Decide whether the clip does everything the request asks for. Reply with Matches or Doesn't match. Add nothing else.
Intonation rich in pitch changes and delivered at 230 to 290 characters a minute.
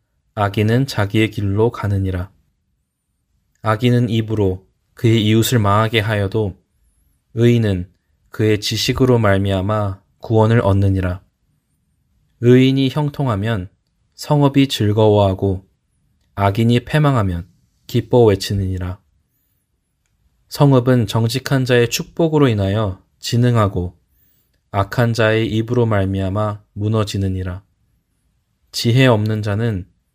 Doesn't match